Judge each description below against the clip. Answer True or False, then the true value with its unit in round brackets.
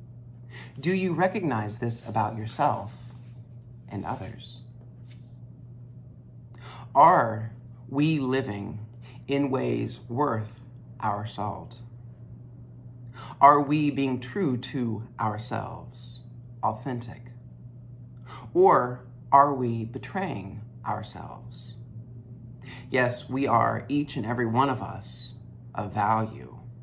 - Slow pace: True (85 wpm)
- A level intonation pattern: True (1.2 semitones)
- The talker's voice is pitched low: True (120 Hz)